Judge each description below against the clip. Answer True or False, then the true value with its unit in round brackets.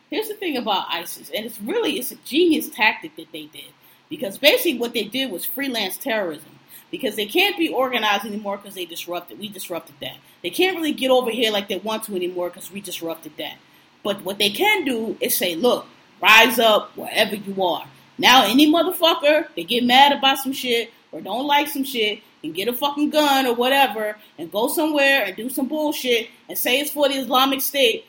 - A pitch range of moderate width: False (6.1 semitones)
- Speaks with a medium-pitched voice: False (250 Hz)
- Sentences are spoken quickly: True (210 wpm)